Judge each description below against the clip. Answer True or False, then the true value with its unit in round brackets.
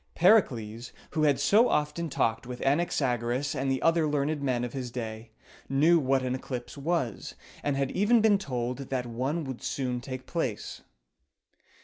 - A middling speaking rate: True (160 wpm)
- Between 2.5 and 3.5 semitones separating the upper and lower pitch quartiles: False (4.2 semitones)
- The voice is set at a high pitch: False (135 Hz)